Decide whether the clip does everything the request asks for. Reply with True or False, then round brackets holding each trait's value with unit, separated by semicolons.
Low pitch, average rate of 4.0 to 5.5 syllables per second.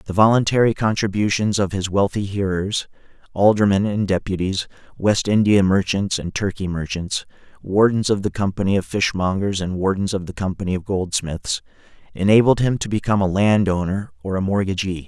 True (100 Hz; 5.4 syllables/s)